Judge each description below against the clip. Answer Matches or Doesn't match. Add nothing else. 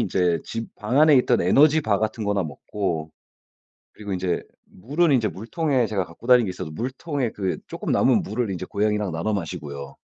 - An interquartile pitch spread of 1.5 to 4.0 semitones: Doesn't match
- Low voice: Matches